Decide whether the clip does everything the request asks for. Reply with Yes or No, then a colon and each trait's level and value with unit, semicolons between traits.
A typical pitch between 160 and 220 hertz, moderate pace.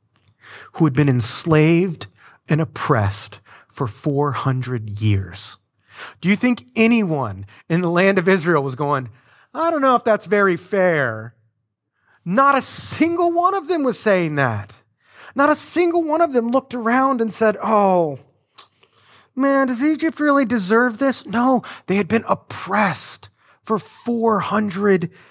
Yes: high, 190 Hz; average, 145 wpm